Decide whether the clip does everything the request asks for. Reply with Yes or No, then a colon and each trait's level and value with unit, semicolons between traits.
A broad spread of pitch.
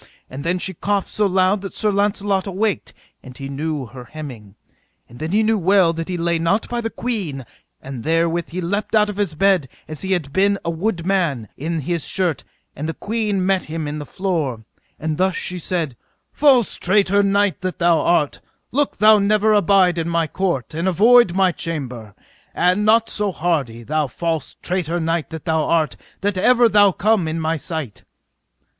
No: average, 4.3 semitones